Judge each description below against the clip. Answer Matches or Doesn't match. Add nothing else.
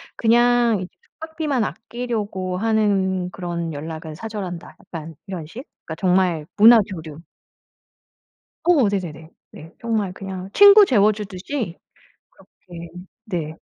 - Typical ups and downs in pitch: Matches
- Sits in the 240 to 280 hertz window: Doesn't match